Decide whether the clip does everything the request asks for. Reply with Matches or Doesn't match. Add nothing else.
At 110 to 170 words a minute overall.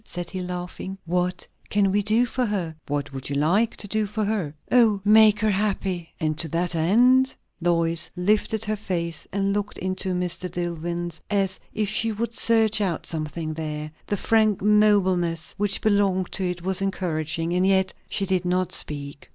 Doesn't match